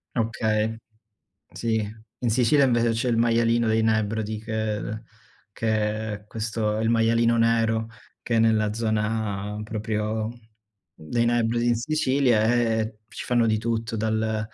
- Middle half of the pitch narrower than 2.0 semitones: Yes, narrow, 1.2 semitones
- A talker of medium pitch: No, low, 110 Hz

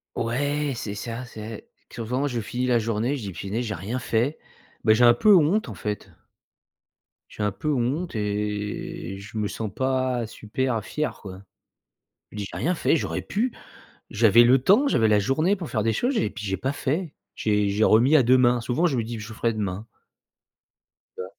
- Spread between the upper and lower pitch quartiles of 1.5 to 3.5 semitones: No, average, 4.2 semitones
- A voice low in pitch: Yes, low, 115 Hz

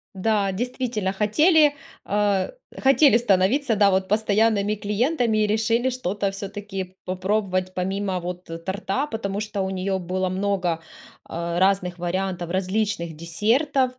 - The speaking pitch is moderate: No, high, 200 Hz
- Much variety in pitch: No, average, 2.8 semitones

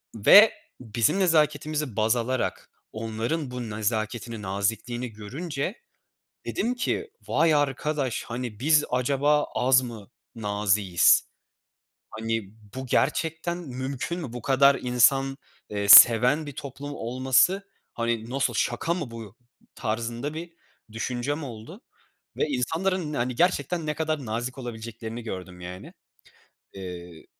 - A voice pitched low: Yes, low, 125 Hz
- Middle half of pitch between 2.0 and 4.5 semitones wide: No, average, 4.9 semitones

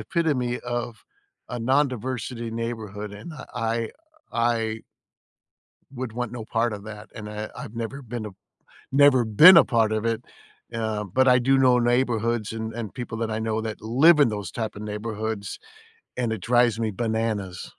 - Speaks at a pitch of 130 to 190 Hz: No, low, 115 Hz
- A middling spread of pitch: No, narrow, 2.2 semitones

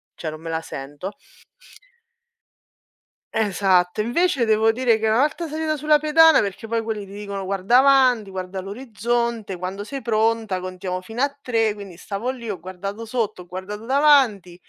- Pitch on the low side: No, high, 215 Hz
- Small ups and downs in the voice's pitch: No, average, 4.7 semitones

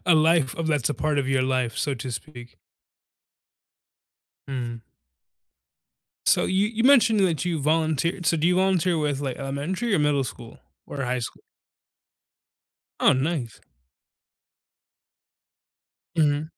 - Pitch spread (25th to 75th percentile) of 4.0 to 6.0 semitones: Yes, average, 4.5 semitones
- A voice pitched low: No, medium, 150 Hz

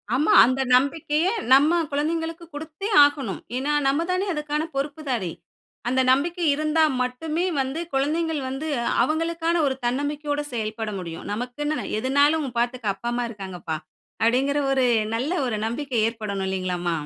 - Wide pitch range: No, average, 4.4 semitones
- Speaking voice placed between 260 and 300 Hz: Yes, very high, 280 Hz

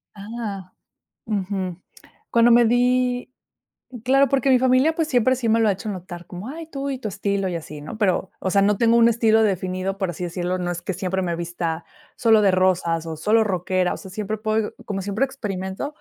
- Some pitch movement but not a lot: Yes, average, 4.2 semitones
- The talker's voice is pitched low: No, high, 200 Hz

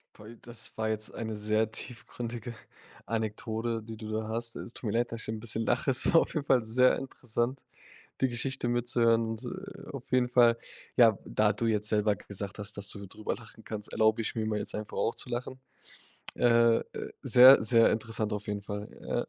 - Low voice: Yes, low, 115 Hz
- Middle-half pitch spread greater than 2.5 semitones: No, narrow, 2.0 semitones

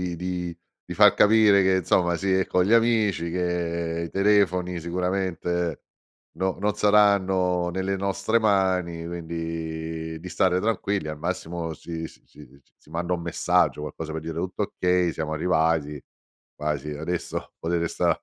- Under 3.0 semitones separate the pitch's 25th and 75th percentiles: Yes, narrow, 2.5 semitones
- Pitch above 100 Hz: No, very low, 90 Hz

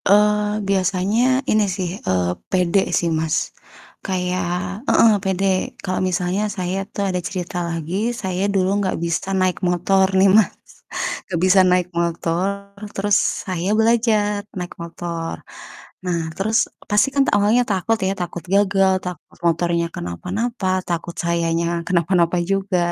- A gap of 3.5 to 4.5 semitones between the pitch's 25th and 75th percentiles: No, narrow, 2.6 semitones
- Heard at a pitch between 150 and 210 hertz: Yes, medium, 185 Hz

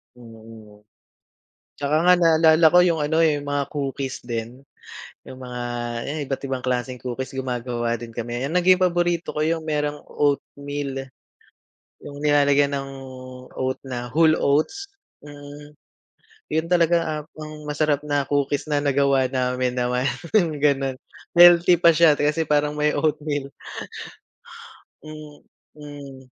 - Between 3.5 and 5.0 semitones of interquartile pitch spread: No, average, 2.9 semitones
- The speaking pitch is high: No, medium, 145 Hz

